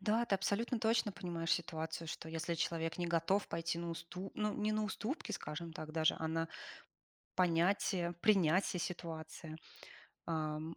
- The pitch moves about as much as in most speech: Yes, average, 3.2 semitones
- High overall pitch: No, medium, 170 Hz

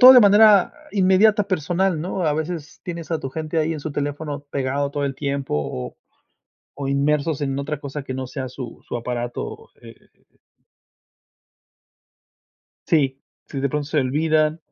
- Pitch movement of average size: Yes, average, 3.2 semitones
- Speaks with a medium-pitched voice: Yes, medium, 150 Hz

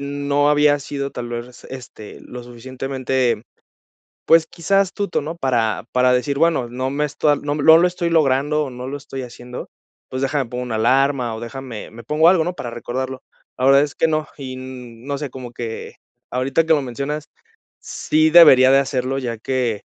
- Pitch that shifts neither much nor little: Yes, average, 3.0 semitones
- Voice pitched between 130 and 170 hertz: Yes, low, 135 Hz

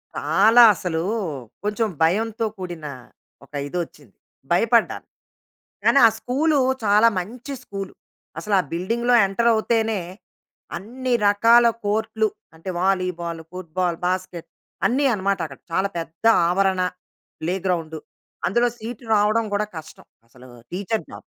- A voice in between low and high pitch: No, high, 200 Hz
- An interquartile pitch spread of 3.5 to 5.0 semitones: Yes, average, 4.2 semitones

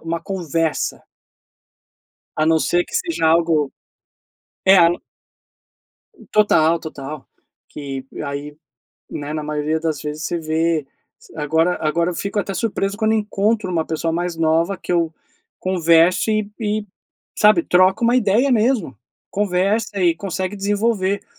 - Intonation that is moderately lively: Yes, average, 4.2 semitones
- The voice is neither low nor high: Yes, medium, 175 Hz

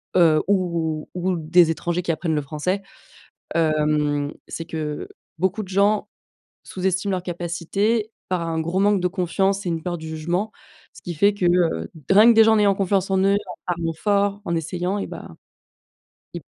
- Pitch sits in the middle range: Yes, medium, 180 Hz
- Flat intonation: No, average, 3.3 semitones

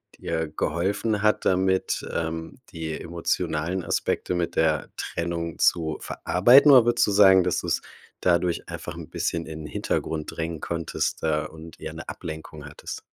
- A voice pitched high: No, very low, 85 Hz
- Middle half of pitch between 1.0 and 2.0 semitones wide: No, average, 2.7 semitones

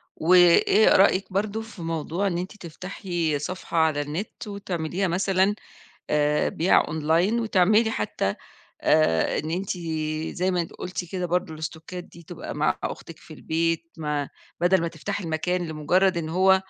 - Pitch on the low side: No, medium, 175 Hz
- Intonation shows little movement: No, average, 3.1 semitones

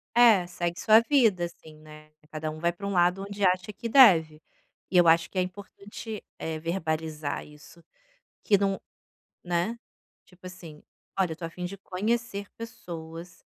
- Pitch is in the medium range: Yes, medium, 180 Hz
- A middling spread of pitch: Yes, average, 3.7 semitones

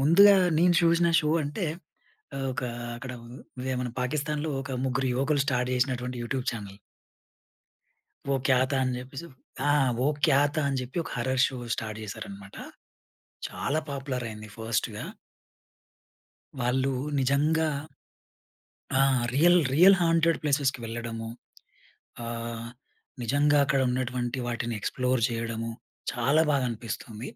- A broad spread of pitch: No, average, 3.5 semitones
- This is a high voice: No, low, 130 Hz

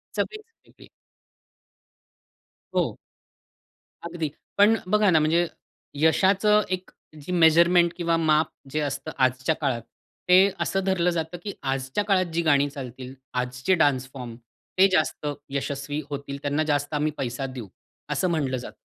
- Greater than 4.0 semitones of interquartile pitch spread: Yes, average, 4.6 semitones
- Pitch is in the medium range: Yes, medium, 155 Hz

